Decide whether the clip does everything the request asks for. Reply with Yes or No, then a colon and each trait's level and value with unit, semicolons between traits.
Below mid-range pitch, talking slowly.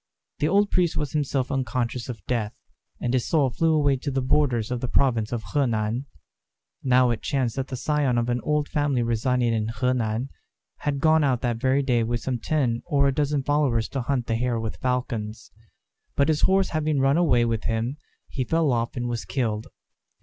No: low, 125 Hz; average, 200 wpm